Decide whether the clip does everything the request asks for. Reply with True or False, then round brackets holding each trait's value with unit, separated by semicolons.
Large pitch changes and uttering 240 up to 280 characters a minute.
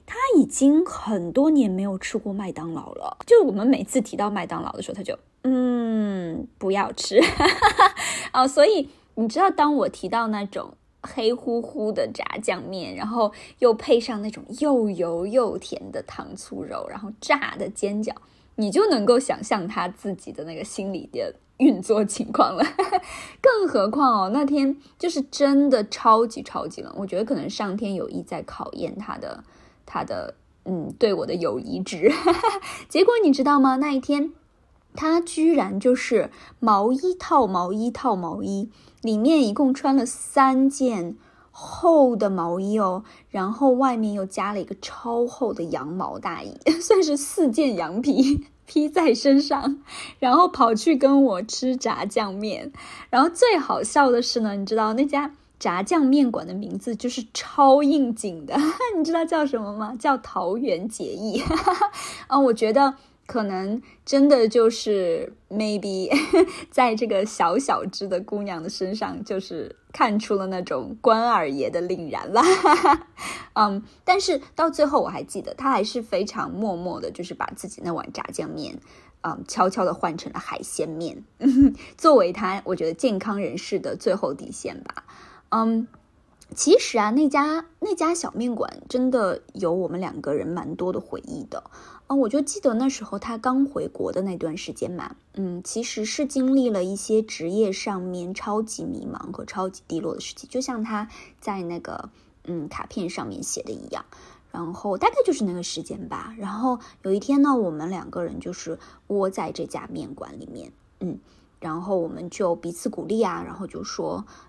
True (6.1 semitones; 245 characters per minute)